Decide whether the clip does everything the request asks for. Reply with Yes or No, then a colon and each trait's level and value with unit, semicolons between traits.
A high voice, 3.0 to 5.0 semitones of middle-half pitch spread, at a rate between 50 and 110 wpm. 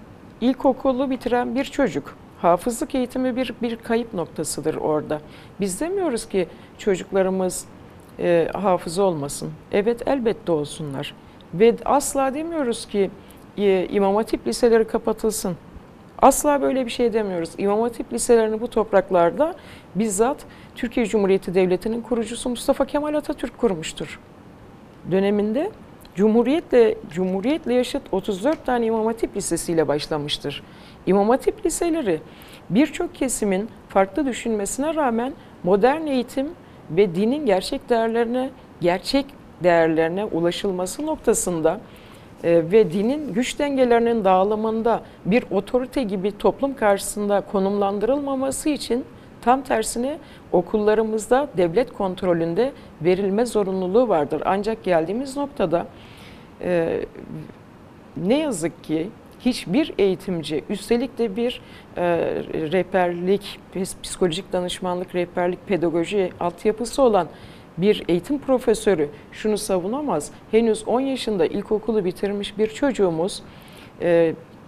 No: high, 215 Hz; wide, 5.5 semitones; average, 105 wpm